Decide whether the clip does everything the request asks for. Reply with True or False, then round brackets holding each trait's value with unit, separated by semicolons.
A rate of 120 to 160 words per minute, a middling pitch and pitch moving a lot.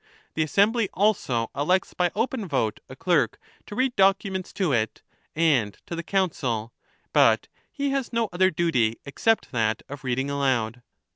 True (155 wpm; 165 Hz; 8.2 semitones)